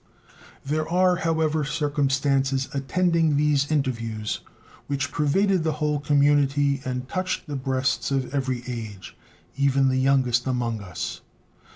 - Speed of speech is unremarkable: No, slow, 125 wpm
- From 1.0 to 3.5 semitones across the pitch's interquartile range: Yes, narrow, 2.5 semitones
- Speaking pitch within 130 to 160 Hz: Yes, medium, 140 Hz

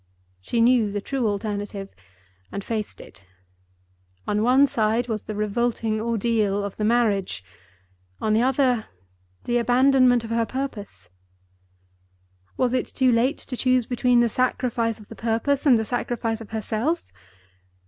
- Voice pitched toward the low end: No, high, 230 Hz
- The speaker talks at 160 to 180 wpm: No, average, 145 wpm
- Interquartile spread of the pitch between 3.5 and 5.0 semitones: No, narrow, 2.6 semitones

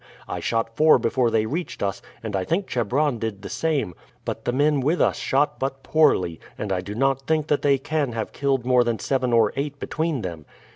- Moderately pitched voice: No, low, 130 Hz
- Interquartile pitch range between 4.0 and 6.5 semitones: Yes, average, 4.6 semitones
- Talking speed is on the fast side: Yes, fast, 220 wpm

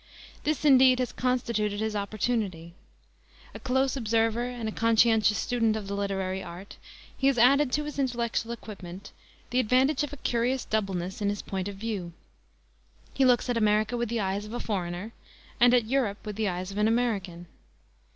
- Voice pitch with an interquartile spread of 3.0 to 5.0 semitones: Yes, average, 3.6 semitones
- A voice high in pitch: Yes, high, 225 Hz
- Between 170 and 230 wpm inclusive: Yes, average, 180 wpm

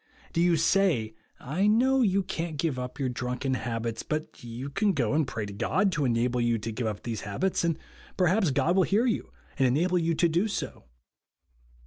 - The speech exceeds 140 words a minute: Yes, average, 200 wpm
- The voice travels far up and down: Yes, wide, 7.2 semitones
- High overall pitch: No, medium, 150 Hz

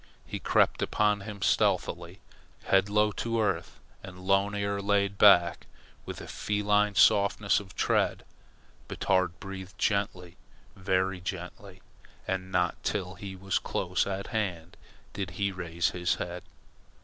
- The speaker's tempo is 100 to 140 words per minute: Yes, slow, 135 wpm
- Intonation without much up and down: Yes, narrow, 1.8 semitones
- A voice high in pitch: No, very low, 95 Hz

